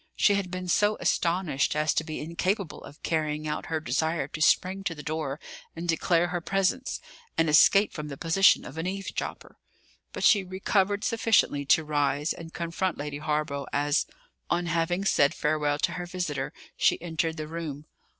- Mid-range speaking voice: Yes, medium, 165 Hz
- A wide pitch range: No, average, 3.4 semitones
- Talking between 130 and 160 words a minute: No, average, 175 wpm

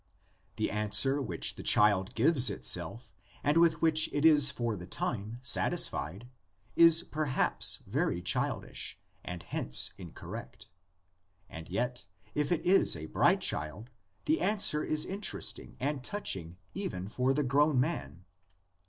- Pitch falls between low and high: No, low, 125 Hz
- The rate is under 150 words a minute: Yes, slow, 135 wpm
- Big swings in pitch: Yes, wide, 8.3 semitones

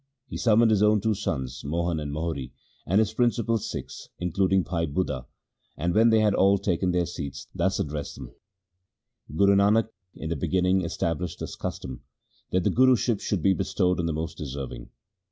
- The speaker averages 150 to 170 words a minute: No, average, 185 wpm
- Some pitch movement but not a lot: Yes, average, 4.4 semitones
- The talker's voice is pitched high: No, very low, 90 Hz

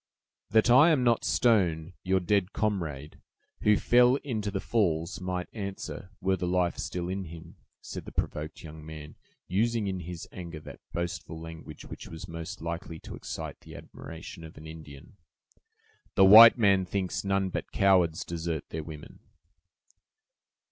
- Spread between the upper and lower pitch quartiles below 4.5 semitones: Yes, average, 3.6 semitones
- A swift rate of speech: No, average, 155 wpm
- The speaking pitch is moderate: No, very low, 90 Hz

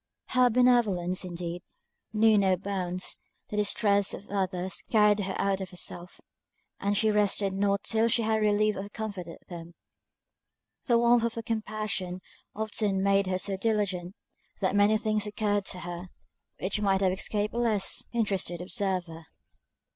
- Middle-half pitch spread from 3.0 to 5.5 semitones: No, narrow, 2.5 semitones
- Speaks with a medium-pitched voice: No, high, 200 Hz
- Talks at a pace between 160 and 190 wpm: No, average, 150 wpm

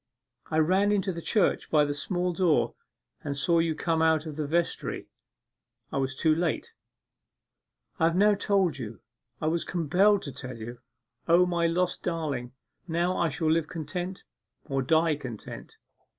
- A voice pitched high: No, medium, 165 Hz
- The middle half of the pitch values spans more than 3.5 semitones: No, average, 3.2 semitones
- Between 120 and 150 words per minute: No, average, 165 wpm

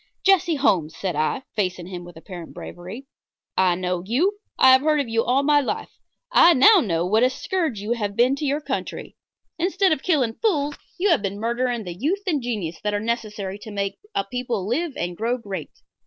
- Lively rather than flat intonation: Yes, wide, 7.0 semitones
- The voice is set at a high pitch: Yes, high, 235 Hz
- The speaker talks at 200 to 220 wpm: Yes, fast, 205 wpm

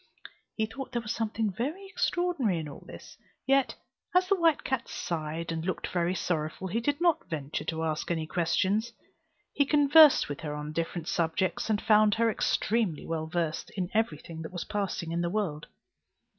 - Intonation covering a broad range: Yes, wide, 6.5 semitones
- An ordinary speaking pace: Yes, average, 185 wpm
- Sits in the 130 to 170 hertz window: No, high, 190 Hz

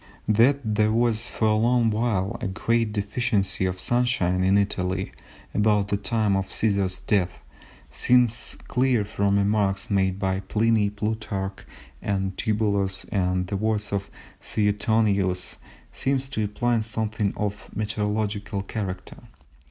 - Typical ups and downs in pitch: No, narrow, 2.3 semitones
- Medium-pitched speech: No, low, 105 Hz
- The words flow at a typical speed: No, slow, 130 wpm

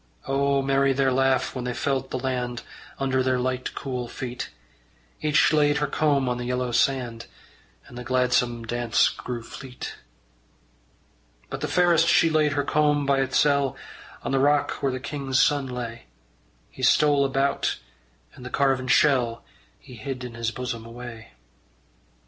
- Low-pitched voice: Yes, low, 130 Hz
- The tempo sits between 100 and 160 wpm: Yes, average, 155 wpm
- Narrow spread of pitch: Yes, narrow, 2.1 semitones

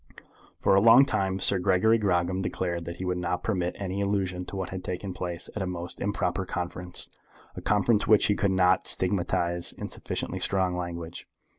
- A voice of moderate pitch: No, very low, 95 Hz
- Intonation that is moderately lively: No, narrow, 1.8 semitones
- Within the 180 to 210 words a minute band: Yes, average, 185 wpm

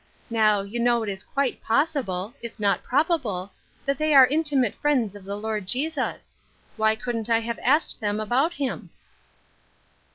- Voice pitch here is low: No, high, 235 Hz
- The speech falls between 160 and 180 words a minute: Yes, average, 170 wpm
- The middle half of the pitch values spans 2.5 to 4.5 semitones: No, average, 4.9 semitones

